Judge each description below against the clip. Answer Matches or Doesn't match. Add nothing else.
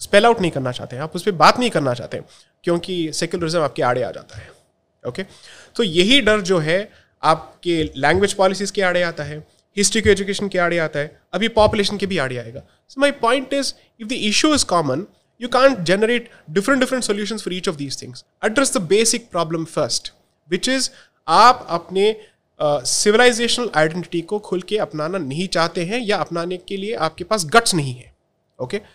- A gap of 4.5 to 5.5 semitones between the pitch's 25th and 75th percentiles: Matches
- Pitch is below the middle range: Doesn't match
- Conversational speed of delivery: Doesn't match